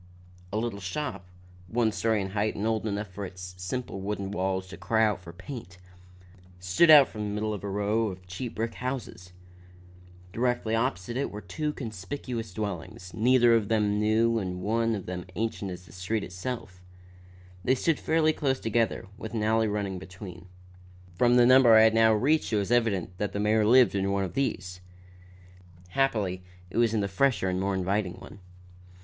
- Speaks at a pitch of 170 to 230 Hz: No, low, 105 Hz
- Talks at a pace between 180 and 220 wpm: Yes, average, 185 wpm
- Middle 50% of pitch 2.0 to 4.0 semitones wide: Yes, average, 3.5 semitones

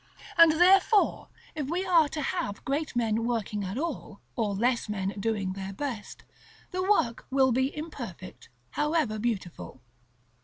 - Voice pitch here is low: No, high, 245 Hz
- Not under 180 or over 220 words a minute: No, average, 145 wpm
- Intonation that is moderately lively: No, wide, 7.0 semitones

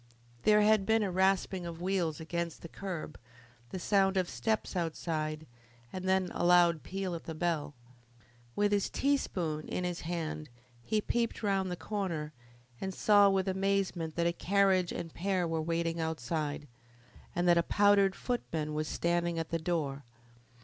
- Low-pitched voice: No, medium, 175 Hz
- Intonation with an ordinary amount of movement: Yes, average, 3.1 semitones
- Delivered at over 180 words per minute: No, average, 165 wpm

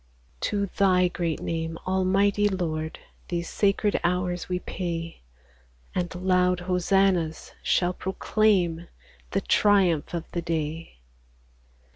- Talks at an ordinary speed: No, slow, 110 wpm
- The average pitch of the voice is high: No, medium, 180 Hz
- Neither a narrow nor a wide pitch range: No, narrow, 2.3 semitones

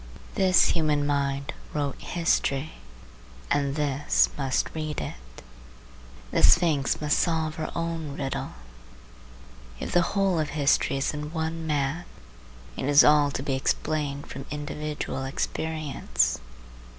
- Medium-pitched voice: Yes, medium, 150 Hz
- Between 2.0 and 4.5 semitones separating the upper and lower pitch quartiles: Yes, narrow, 2.4 semitones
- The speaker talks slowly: Yes, slow, 125 wpm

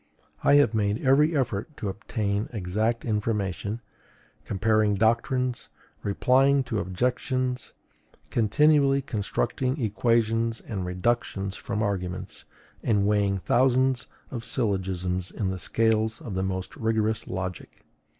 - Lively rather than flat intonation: No, average, 4.1 semitones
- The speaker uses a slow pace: Yes, slow, 110 wpm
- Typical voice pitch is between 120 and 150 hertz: No, low, 110 Hz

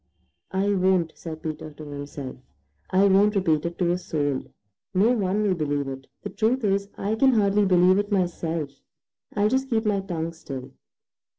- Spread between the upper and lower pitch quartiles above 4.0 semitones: Yes, average, 4.5 semitones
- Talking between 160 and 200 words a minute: Yes, average, 175 wpm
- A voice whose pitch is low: No, medium, 185 Hz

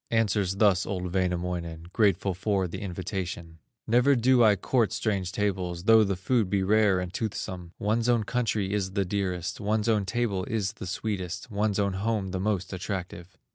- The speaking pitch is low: Yes, low, 100 Hz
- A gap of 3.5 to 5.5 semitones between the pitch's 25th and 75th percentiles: No, average, 3.0 semitones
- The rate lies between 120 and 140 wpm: No, average, 175 wpm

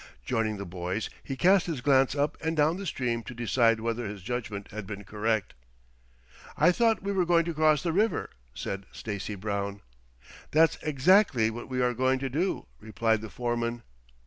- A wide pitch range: Yes, wide, 6.3 semitones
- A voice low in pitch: Yes, low, 120 Hz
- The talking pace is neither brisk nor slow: Yes, average, 180 wpm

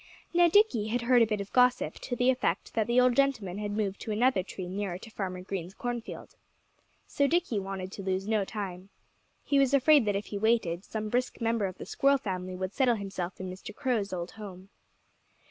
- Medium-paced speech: No, fast, 210 wpm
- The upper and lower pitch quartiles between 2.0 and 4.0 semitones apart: No, average, 4.5 semitones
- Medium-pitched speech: No, high, 210 Hz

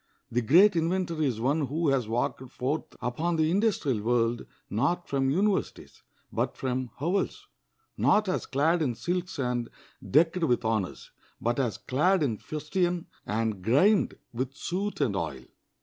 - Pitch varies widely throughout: Yes, wide, 6.3 semitones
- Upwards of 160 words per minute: No, average, 150 wpm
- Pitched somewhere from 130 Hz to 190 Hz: Yes, medium, 140 Hz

